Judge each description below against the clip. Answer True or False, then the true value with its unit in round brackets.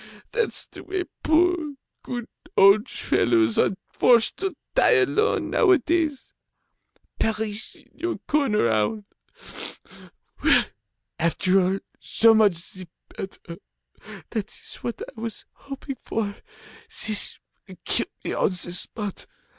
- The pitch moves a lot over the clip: True (7.8 semitones)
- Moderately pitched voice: False (220 Hz)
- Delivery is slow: True (120 wpm)